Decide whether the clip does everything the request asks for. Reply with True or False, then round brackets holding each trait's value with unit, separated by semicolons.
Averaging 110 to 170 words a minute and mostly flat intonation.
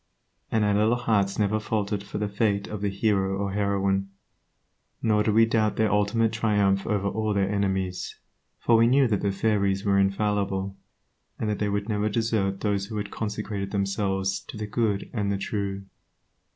False (180 wpm; 1.6 semitones)